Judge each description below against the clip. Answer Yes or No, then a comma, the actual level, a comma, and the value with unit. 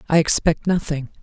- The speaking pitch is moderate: Yes, medium, 160 Hz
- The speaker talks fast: No, average, 145 wpm